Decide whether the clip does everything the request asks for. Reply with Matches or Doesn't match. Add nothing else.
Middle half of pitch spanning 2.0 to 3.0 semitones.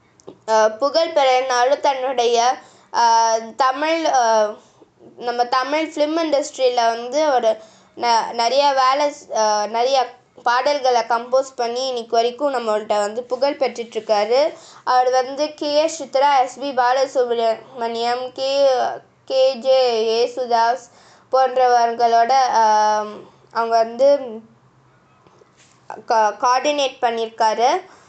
Matches